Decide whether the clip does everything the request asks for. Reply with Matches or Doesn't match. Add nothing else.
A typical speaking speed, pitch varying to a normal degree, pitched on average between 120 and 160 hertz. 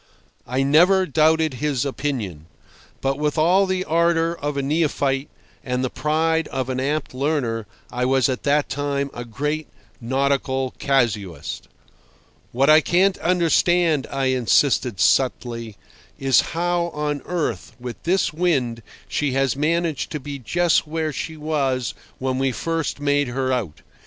Matches